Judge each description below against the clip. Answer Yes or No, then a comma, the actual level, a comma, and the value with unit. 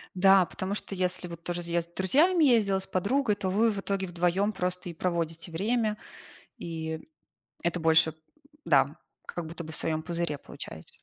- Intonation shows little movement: No, average, 3.1 semitones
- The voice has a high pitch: No, medium, 180 Hz